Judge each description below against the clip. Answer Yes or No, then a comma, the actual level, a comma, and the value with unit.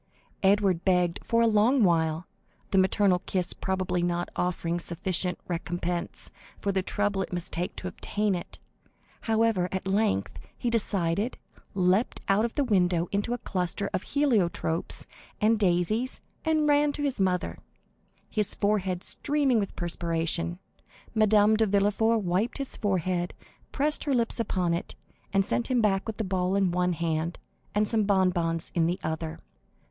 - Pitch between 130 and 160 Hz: No, high, 190 Hz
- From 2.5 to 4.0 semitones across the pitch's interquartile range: Yes, average, 3.7 semitones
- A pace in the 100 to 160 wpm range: Yes, average, 155 wpm